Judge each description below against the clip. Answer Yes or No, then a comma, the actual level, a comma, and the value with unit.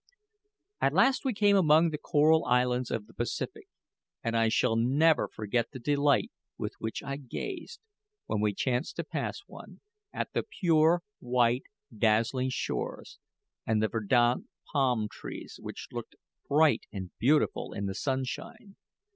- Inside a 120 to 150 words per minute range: Yes, average, 145 wpm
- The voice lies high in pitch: No, low, 130 Hz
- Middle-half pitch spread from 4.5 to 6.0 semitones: Yes, wide, 5.6 semitones